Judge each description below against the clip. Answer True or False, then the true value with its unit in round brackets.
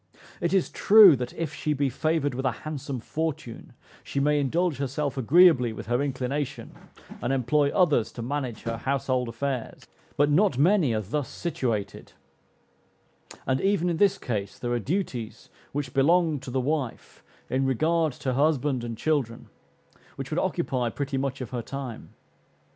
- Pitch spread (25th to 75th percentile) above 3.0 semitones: True (3.8 semitones)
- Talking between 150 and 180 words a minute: True (165 wpm)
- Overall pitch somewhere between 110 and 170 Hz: True (140 Hz)